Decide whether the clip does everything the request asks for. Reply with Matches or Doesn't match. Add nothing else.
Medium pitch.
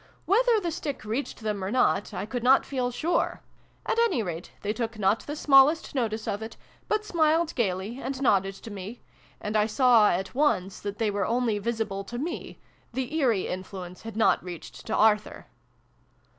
Doesn't match